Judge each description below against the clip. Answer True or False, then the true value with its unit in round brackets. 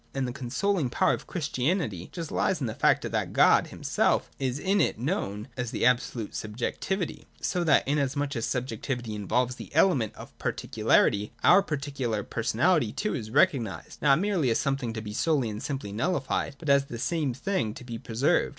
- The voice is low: True (130 Hz)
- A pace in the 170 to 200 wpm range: True (185 wpm)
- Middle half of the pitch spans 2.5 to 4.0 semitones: False (4.7 semitones)